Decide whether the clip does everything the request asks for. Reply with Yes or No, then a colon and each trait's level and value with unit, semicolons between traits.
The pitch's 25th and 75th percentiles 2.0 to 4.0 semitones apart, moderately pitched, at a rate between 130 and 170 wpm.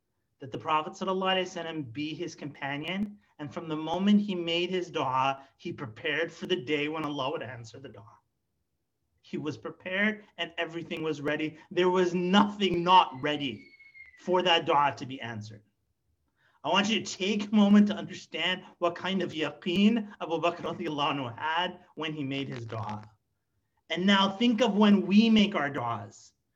No: average, 4.8 semitones; medium, 165 Hz; average, 165 wpm